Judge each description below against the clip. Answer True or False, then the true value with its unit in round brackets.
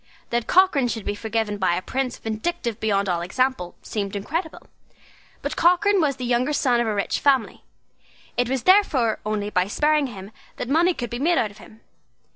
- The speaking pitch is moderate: False (240 Hz)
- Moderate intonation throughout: False (5.9 semitones)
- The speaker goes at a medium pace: True (190 wpm)